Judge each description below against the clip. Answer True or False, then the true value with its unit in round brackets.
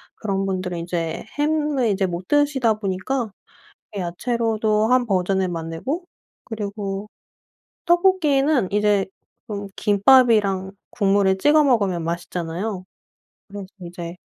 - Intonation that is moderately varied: True (4.9 semitones)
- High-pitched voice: True (205 Hz)